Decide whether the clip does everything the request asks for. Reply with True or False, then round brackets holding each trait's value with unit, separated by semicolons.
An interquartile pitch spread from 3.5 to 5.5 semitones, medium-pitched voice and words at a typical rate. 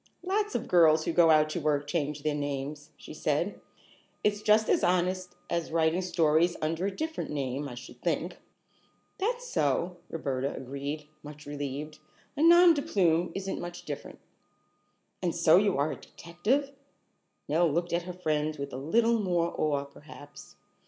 True (3.8 semitones; 165 Hz; 165 wpm)